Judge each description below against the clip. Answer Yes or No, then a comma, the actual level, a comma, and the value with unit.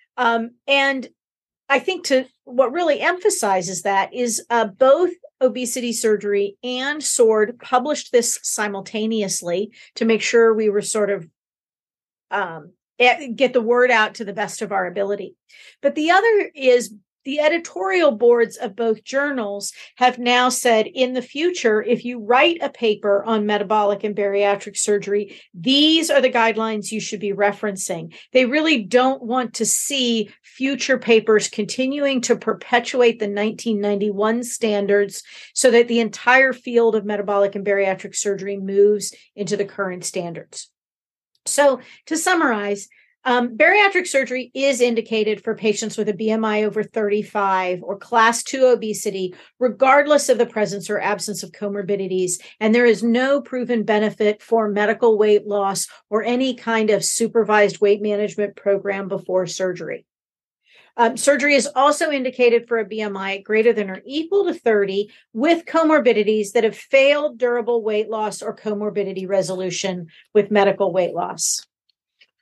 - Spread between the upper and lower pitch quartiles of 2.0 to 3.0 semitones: No, average, 3.8 semitones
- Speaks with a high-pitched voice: Yes, high, 225 Hz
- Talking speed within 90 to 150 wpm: Yes, average, 145 wpm